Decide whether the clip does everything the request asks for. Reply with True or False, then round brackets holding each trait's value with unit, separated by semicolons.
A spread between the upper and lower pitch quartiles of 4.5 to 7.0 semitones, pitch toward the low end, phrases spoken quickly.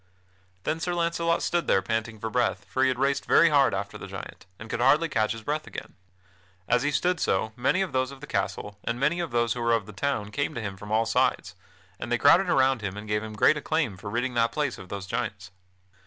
True (5.5 semitones; 120 Hz; 245 wpm)